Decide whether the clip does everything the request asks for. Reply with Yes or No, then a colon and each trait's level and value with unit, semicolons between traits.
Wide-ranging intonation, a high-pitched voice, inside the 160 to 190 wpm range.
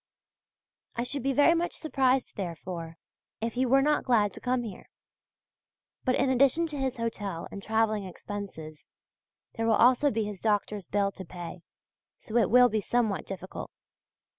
No: average, 4.5 semitones; high, 225 Hz; average, 165 wpm